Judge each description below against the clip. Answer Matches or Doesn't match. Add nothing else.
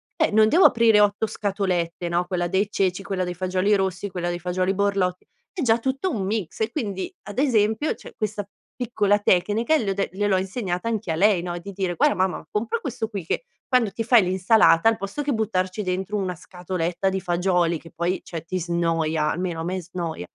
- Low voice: Doesn't match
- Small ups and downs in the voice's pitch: Doesn't match